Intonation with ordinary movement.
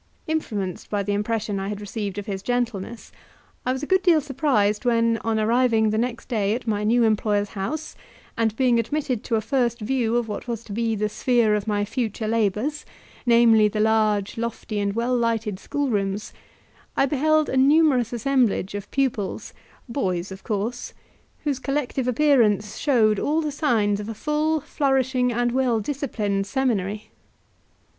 Yes: average, 3.8 semitones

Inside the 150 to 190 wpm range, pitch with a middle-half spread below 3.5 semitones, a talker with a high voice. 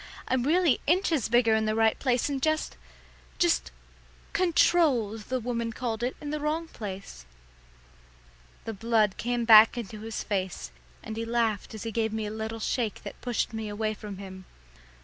Yes: average, 170 wpm; average, 2.8 semitones; high, 225 Hz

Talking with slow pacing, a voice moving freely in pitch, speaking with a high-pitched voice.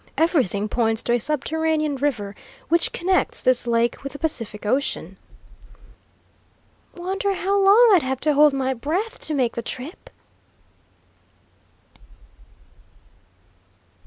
Yes: slow, 115 wpm; wide, 6.0 semitones; very high, 285 Hz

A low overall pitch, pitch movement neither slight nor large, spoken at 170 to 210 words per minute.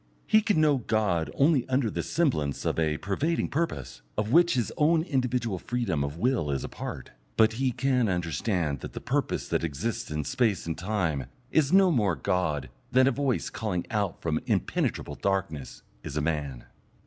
No: low, 105 Hz; wide, 8.5 semitones; average, 180 wpm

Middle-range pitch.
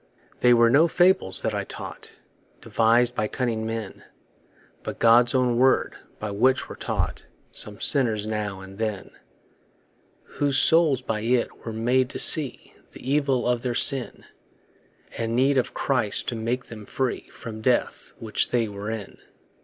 No: low, 120 Hz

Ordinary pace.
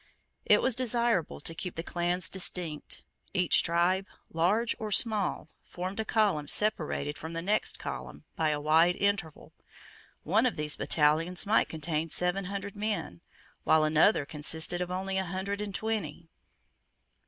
Yes: average, 150 wpm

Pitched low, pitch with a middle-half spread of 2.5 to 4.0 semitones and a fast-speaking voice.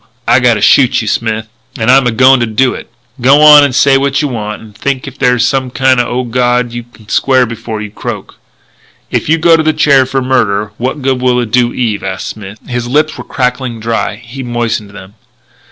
Yes: low, 125 Hz; average, 2.9 semitones; fast, 215 wpm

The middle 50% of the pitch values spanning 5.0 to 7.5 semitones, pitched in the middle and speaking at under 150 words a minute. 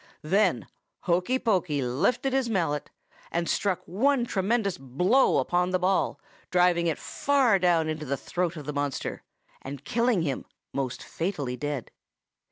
Yes: wide, 5.5 semitones; medium, 175 Hz; average, 140 wpm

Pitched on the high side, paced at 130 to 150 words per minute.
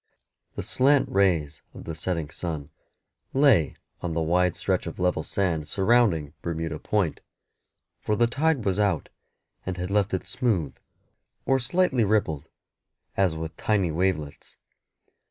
No: very low, 90 Hz; slow, 135 wpm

